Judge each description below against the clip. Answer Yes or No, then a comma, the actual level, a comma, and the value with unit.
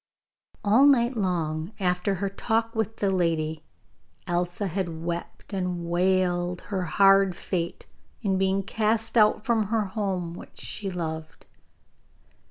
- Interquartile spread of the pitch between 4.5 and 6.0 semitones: No, average, 3.3 semitones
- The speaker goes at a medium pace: No, slow, 130 wpm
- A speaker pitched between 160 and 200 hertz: Yes, high, 190 Hz